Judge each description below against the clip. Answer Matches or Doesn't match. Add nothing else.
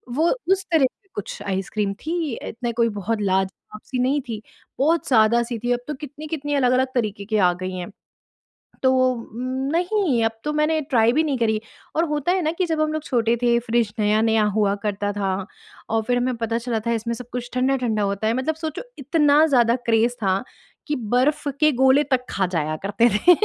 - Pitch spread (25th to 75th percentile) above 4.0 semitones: Matches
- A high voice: Matches